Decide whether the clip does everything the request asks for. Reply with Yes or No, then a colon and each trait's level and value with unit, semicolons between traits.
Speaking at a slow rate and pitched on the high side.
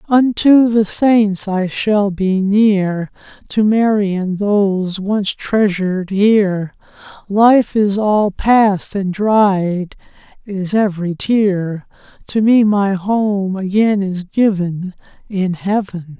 Yes: slow, 120 wpm; high, 200 Hz